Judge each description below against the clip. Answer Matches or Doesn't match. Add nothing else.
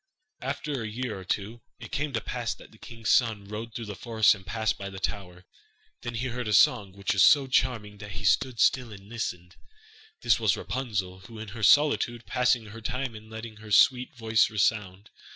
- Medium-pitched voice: Doesn't match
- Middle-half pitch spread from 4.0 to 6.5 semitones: Doesn't match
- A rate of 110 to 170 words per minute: Doesn't match